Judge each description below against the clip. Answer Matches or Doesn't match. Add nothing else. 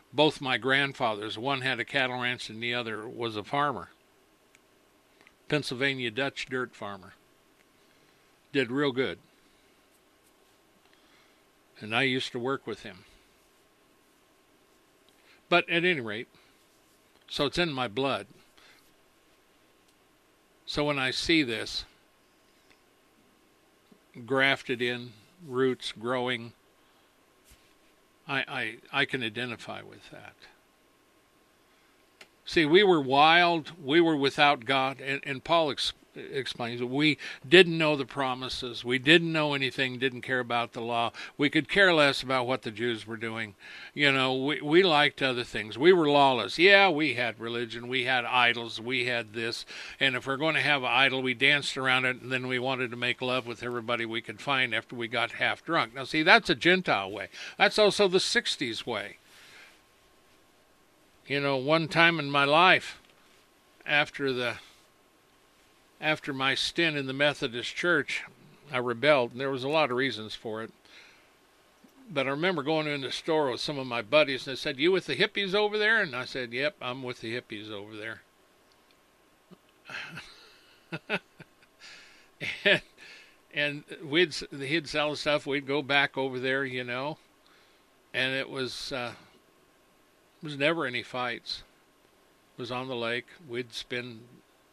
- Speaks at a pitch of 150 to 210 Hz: Doesn't match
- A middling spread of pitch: Matches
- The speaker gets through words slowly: Doesn't match